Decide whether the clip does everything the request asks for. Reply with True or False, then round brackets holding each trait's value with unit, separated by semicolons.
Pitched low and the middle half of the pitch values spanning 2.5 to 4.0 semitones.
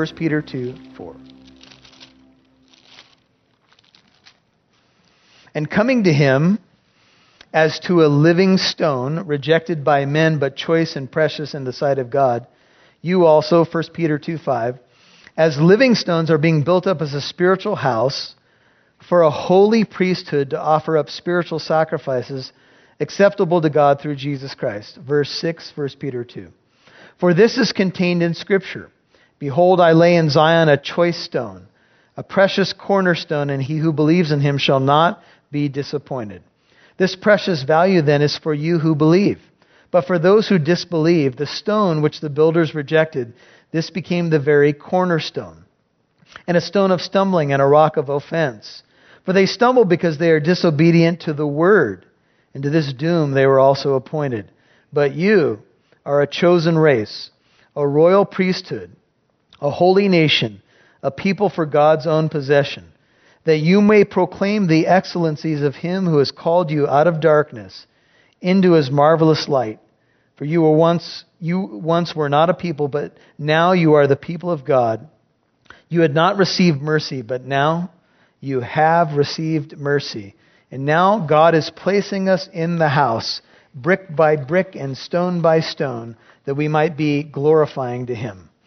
False (155 Hz; 3.5 semitones)